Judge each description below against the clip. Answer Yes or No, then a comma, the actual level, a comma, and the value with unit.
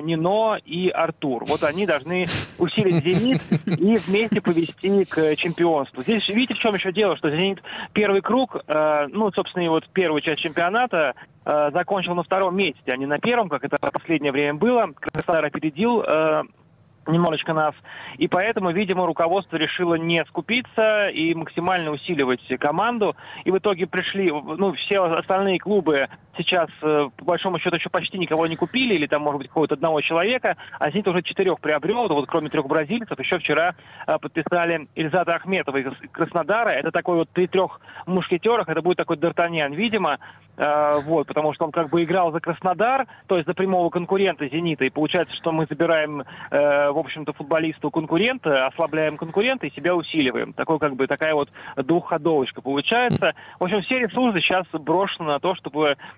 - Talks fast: Yes, fast, 170 wpm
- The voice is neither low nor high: Yes, medium, 170 Hz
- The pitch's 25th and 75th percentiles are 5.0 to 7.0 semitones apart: No, average, 3.7 semitones